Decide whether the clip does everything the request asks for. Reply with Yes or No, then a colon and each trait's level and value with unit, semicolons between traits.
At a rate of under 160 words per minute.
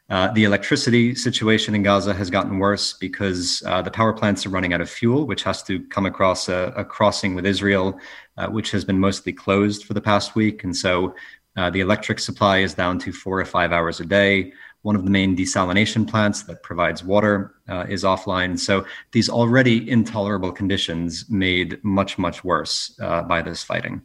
No: average, 195 wpm